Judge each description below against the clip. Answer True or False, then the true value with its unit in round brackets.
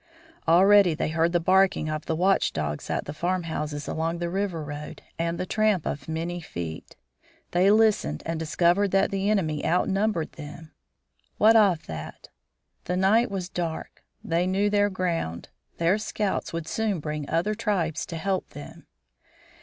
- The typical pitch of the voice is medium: True (175 Hz)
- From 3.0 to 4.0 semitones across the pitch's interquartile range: True (3.6 semitones)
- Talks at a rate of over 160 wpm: False (155 wpm)